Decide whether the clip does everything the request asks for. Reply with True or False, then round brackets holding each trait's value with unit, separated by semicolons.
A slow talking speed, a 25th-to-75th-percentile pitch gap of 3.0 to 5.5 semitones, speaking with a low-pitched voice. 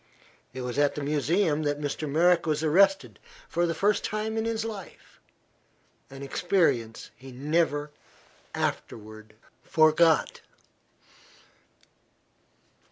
False (105 wpm; 4.3 semitones; 155 Hz)